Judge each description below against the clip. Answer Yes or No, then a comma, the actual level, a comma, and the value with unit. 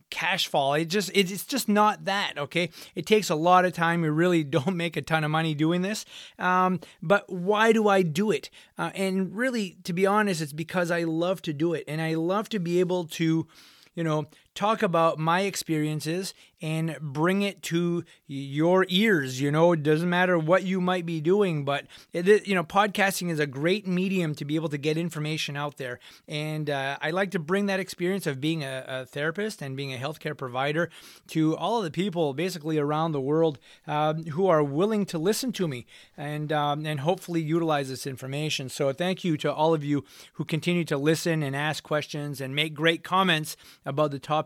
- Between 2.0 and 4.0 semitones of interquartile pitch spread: Yes, average, 3.5 semitones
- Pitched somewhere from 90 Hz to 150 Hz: No, medium, 165 Hz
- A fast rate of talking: Yes, fast, 210 wpm